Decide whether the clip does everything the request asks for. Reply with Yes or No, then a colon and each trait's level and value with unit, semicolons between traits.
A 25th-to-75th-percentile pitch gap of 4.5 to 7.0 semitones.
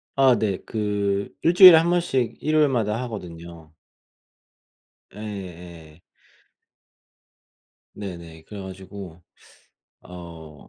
Yes: average, 5.2 semitones